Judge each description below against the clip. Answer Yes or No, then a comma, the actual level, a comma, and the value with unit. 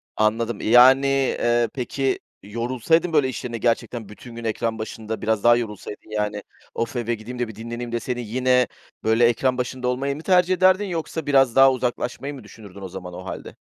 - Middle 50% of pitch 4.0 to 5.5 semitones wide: No, average, 3.0 semitones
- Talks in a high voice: No, low, 120 Hz